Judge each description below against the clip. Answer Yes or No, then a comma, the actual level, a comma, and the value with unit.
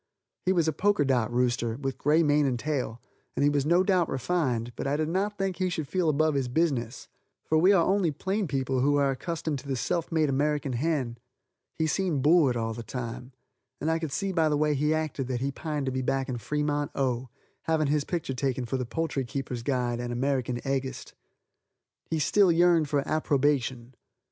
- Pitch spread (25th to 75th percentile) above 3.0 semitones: Yes, average, 3.7 semitones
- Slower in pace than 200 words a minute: No, fast, 205 wpm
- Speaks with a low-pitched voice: No, medium, 145 Hz